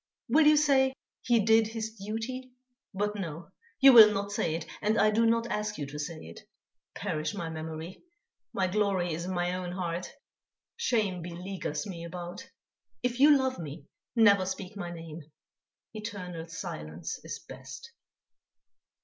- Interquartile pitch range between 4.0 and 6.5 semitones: Yes, average, 4.8 semitones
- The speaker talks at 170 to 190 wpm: No, average, 155 wpm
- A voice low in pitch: No, high, 190 Hz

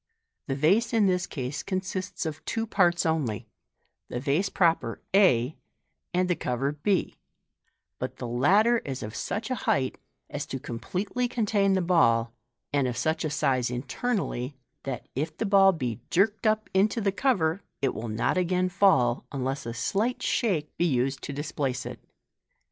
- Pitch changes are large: Yes, wide, 7.1 semitones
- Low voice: No, medium, 160 Hz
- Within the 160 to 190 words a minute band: Yes, average, 165 wpm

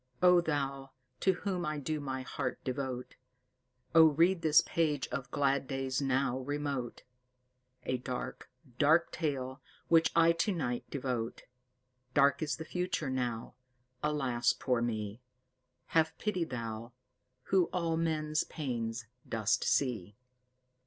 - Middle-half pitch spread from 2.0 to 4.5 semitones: Yes, average, 4.1 semitones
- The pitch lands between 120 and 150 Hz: Yes, medium, 140 Hz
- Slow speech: Yes, slow, 125 wpm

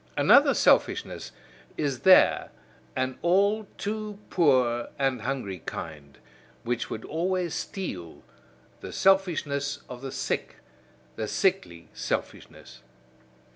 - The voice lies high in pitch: No, medium, 140 Hz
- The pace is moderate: No, slow, 100 wpm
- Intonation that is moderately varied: No, wide, 7.9 semitones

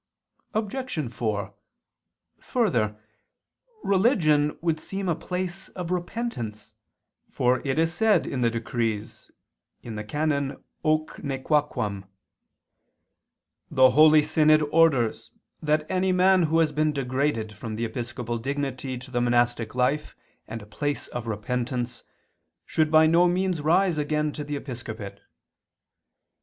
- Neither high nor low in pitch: Yes, medium, 145 Hz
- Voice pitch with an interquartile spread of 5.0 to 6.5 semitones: Yes, average, 5.3 semitones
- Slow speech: Yes, slow, 125 wpm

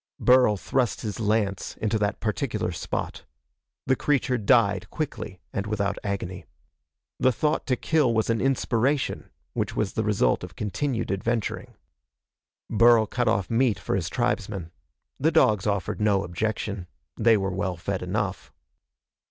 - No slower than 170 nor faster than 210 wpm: No, average, 145 wpm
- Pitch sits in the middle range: No, low, 110 Hz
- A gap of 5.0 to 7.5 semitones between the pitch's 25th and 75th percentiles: No, average, 3.4 semitones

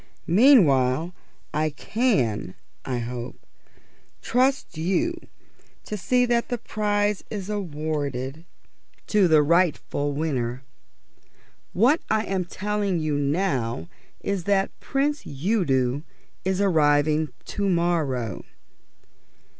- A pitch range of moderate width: No, wide, 6.5 semitones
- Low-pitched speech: No, medium, 170 Hz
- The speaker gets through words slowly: Yes, slow, 100 wpm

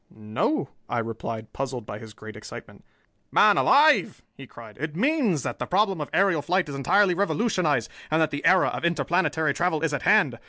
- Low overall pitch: No, medium, 160 Hz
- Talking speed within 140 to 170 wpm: No, average, 190 wpm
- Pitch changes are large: Yes, wide, 7.5 semitones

